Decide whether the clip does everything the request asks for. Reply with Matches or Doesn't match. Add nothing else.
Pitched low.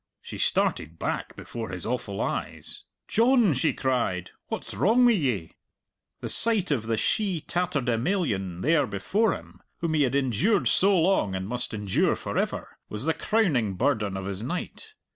Matches